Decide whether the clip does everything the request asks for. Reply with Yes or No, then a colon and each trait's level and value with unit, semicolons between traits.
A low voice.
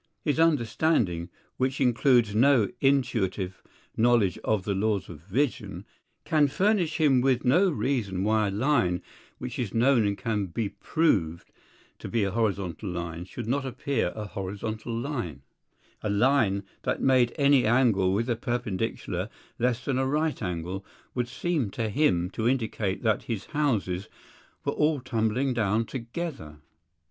Yes: low, 115 Hz